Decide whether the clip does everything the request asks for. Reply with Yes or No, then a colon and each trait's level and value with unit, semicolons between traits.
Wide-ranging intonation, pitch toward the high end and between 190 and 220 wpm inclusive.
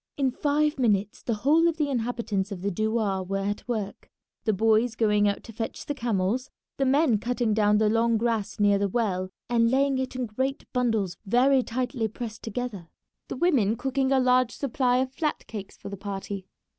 No: average, 3.8 semitones; high, 230 Hz; average, 195 wpm